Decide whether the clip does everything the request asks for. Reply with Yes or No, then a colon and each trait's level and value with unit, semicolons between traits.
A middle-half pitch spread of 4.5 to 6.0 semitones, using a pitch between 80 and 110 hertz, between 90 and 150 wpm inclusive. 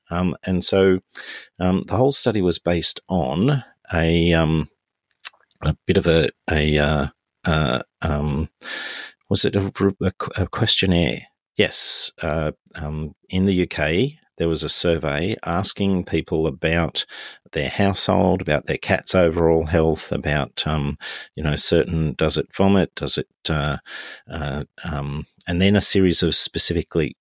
No: average, 3.4 semitones; very low, 85 Hz; average, 140 wpm